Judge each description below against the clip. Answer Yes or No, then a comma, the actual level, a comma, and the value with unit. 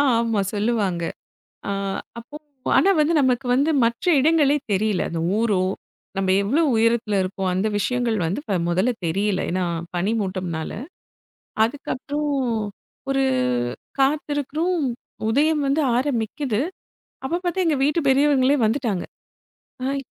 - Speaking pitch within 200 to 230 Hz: No, high, 240 Hz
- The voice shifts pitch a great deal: Yes, wide, 6.1 semitones